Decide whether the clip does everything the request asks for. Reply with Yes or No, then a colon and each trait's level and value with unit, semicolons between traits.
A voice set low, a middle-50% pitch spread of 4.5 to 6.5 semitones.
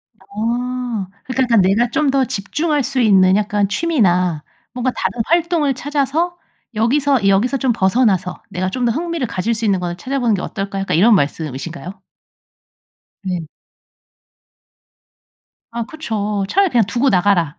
No: high, 225 Hz; wide, 5.4 semitones